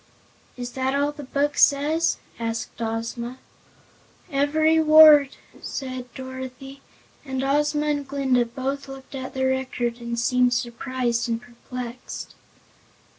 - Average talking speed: No, slow, 125 wpm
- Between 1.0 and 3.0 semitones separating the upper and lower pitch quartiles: Yes, narrow, 2.5 semitones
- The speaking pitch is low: No, very high, 260 Hz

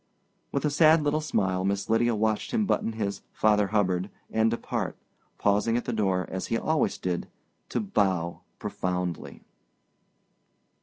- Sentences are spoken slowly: No, average, 145 wpm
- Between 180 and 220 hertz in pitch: No, low, 105 Hz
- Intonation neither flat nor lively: Yes, average, 4.0 semitones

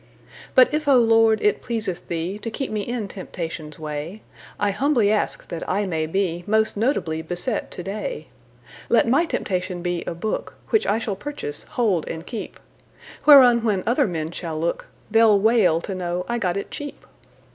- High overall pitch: Yes, high, 205 Hz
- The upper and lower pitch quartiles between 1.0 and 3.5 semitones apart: No, average, 5.1 semitones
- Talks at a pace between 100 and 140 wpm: No, average, 155 wpm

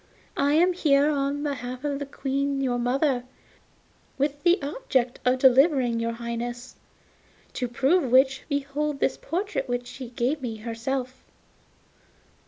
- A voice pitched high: Yes, very high, 270 Hz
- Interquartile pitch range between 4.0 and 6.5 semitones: No, average, 2.7 semitones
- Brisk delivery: No, slow, 135 wpm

